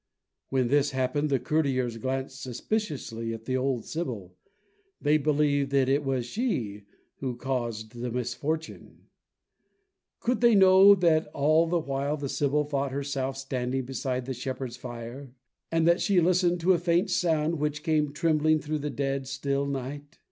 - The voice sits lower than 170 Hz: Yes, medium, 140 Hz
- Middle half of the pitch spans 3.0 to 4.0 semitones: Yes, average, 3.4 semitones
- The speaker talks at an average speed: Yes, average, 155 wpm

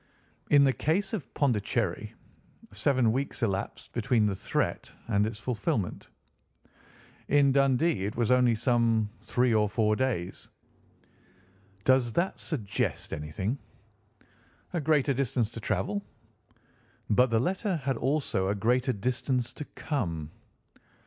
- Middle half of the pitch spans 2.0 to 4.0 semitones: No, average, 4.4 semitones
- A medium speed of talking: No, slow, 125 wpm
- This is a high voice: No, low, 120 Hz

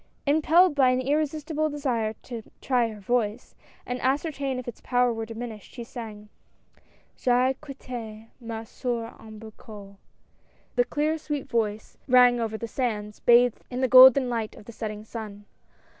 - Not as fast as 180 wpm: Yes, average, 160 wpm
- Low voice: No, high, 245 Hz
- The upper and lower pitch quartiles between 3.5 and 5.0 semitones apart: No, average, 3.0 semitones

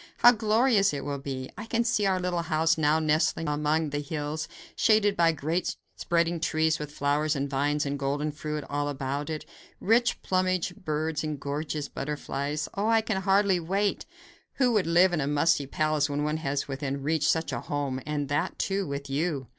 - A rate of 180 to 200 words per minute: Yes, average, 190 wpm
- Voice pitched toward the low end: No, medium, 155 Hz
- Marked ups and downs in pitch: No, average, 3.9 semitones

